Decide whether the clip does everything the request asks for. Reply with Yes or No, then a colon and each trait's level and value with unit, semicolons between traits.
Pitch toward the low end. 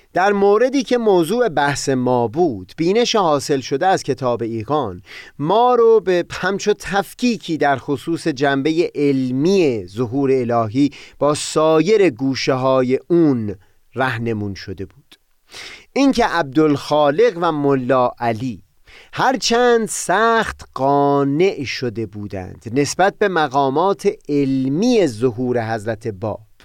No: medium, 145 Hz